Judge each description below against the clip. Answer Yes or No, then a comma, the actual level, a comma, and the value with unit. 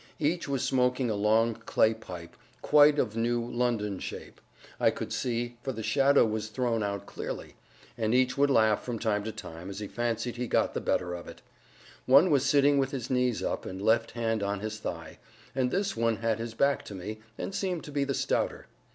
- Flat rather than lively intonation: No, average, 3.6 semitones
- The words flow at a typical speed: No, fast, 210 wpm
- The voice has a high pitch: No, low, 115 Hz